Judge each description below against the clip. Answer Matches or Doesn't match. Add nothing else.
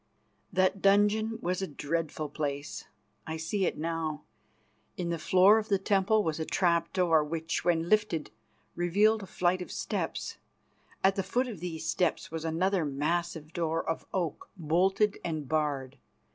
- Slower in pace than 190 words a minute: Matches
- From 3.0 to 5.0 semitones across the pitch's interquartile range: Matches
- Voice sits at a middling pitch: Matches